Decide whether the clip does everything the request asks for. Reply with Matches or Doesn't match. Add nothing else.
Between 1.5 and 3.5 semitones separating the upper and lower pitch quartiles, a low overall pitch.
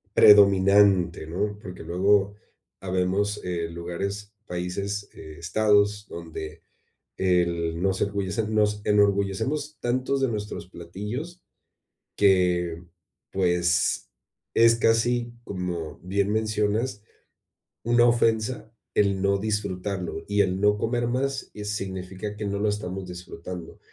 Matches